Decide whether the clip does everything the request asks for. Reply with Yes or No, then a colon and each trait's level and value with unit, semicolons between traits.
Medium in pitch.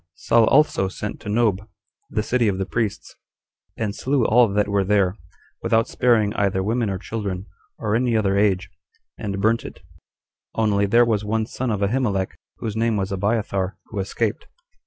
No: low, 105 Hz